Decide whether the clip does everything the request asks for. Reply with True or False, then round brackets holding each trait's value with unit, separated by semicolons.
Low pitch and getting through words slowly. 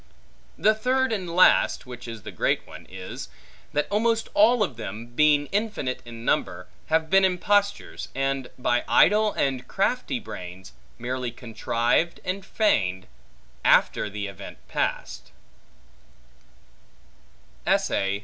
False (145 Hz; 120 wpm)